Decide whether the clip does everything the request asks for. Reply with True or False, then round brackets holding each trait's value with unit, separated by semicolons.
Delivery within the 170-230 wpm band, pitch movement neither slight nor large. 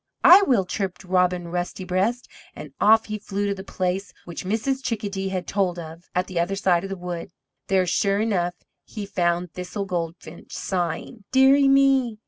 True (180 wpm; 3.2 semitones)